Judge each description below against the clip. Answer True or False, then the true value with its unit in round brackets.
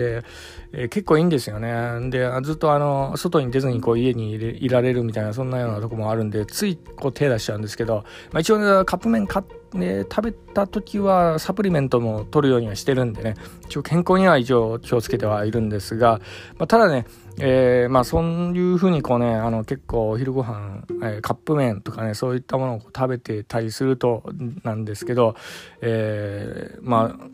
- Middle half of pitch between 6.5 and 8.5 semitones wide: False (5.5 semitones)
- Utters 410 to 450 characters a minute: False (395 characters per minute)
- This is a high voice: False (125 Hz)